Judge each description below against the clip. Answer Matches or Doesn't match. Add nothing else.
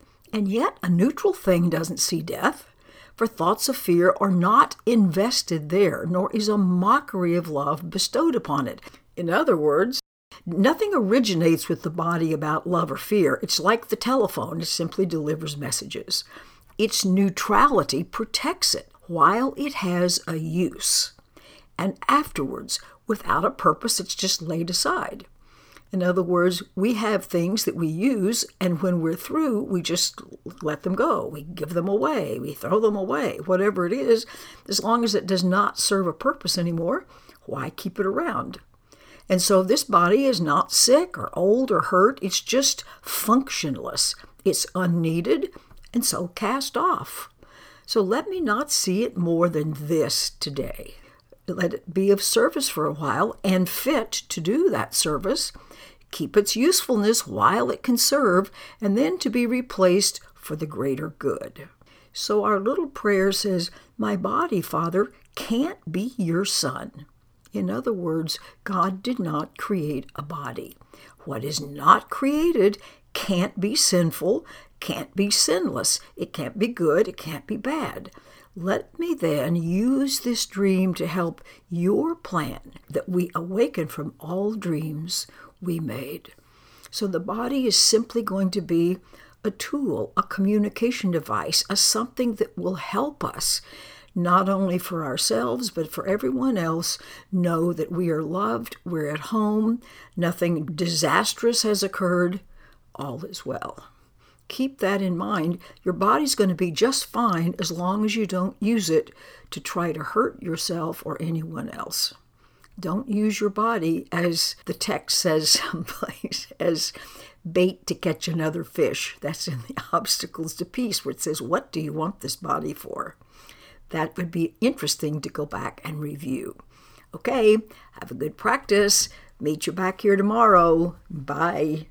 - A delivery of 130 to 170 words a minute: Matches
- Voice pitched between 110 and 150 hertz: Doesn't match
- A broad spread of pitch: Doesn't match